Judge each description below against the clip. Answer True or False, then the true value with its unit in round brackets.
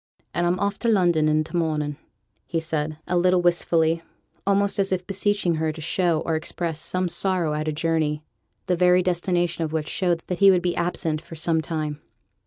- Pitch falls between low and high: True (170 Hz)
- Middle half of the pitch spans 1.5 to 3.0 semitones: True (2.4 semitones)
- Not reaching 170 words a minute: False (195 wpm)